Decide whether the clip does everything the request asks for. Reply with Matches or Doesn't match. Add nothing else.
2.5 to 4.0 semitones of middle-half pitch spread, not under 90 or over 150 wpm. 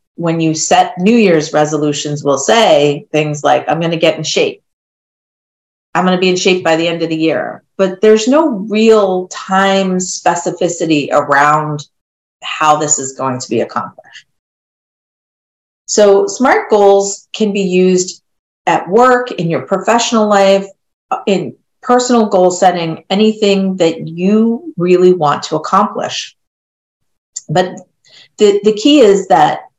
Doesn't match